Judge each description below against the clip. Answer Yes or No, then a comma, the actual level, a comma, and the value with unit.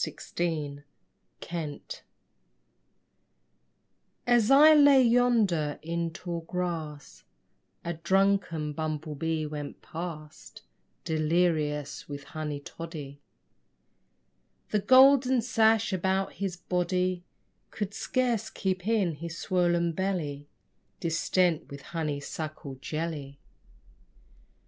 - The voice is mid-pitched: Yes, medium, 170 Hz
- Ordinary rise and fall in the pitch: Yes, average, 4.2 semitones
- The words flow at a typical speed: No, slow, 90 wpm